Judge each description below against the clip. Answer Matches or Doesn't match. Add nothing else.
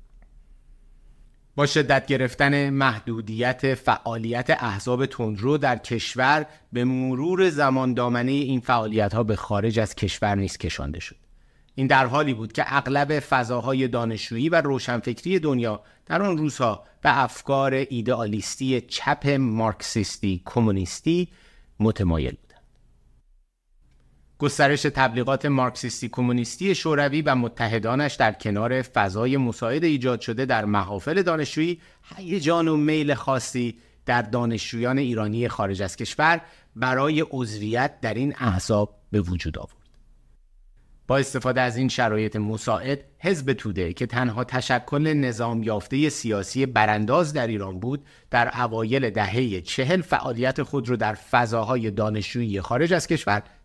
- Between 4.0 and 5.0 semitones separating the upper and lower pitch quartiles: Matches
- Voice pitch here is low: Matches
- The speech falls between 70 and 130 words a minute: Matches